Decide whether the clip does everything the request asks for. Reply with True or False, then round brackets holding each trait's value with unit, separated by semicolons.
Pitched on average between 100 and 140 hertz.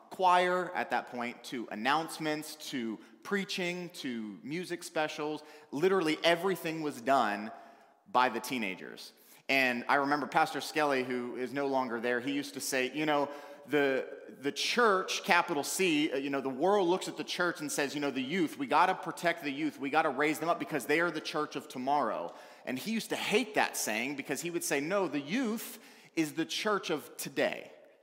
False (155 Hz)